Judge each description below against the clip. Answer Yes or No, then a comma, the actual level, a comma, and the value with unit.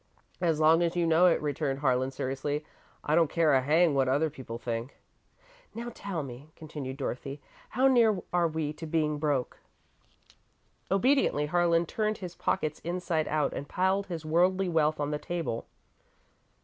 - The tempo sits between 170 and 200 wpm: No, average, 160 wpm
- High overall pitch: No, medium, 155 Hz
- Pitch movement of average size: Yes, average, 3.5 semitones